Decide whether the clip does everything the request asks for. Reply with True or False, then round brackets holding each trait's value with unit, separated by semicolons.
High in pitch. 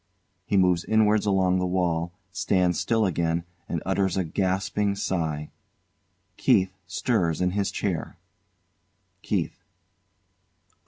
False (95 Hz)